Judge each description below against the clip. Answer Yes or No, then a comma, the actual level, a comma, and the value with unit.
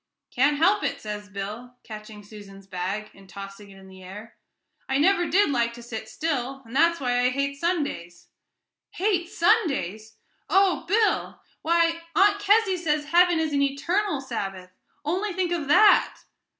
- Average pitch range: No, wide, 8.6 semitones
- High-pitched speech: Yes, very high, 280 Hz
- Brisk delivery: No, average, 160 wpm